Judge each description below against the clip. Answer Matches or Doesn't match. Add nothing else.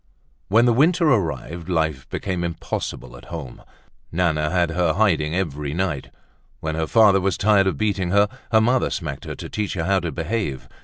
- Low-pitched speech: Matches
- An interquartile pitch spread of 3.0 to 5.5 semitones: Matches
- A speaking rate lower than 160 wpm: Doesn't match